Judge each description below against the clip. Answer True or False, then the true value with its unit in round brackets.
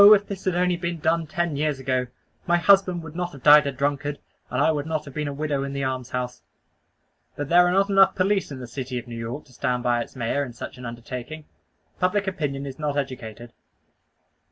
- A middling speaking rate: False (225 wpm)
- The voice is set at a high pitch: False (145 Hz)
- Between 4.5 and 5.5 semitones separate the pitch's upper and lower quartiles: True (5.2 semitones)